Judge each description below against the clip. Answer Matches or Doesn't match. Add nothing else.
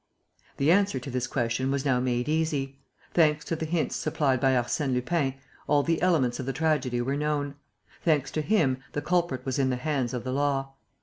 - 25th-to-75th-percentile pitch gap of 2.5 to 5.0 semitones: Matches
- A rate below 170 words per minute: Doesn't match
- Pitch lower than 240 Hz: Matches